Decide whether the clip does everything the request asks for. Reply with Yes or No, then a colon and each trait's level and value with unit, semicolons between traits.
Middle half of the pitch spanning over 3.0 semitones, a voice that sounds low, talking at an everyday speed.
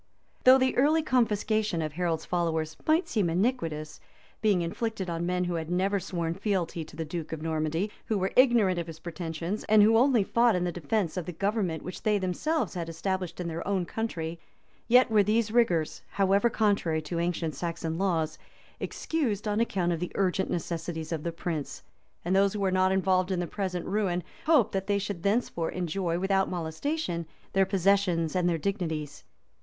No: average, 3.8 semitones; medium, 185 Hz; average, 185 wpm